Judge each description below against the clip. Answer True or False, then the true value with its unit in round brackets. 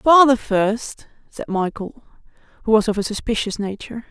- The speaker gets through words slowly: False (145 wpm)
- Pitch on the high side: True (220 Hz)